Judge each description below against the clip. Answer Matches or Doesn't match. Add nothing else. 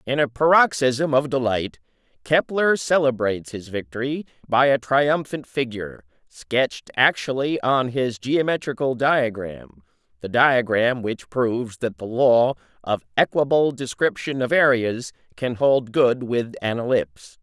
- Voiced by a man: Matches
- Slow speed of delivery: Matches